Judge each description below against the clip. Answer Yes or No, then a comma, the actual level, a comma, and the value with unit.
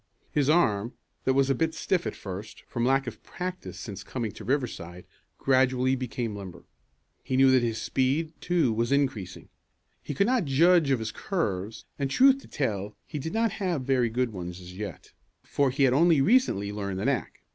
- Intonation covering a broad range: Yes, wide, 5.9 semitones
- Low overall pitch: Yes, low, 130 Hz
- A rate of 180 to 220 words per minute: Yes, average, 190 wpm